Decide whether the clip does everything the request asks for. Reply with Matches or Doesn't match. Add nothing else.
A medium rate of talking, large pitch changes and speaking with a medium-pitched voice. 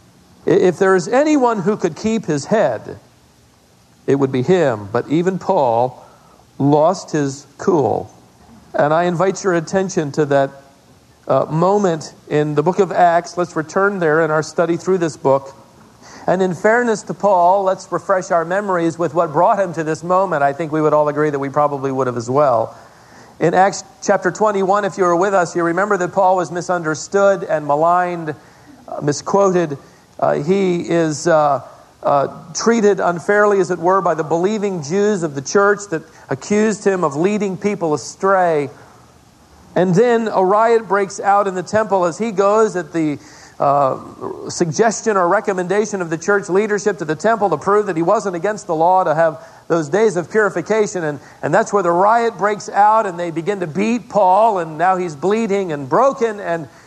Doesn't match